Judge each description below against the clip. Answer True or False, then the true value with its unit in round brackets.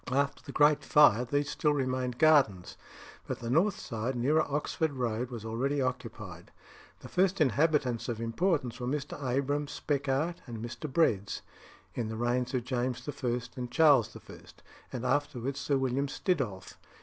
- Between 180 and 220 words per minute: False (155 wpm)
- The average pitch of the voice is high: False (130 Hz)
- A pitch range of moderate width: True (3.4 semitones)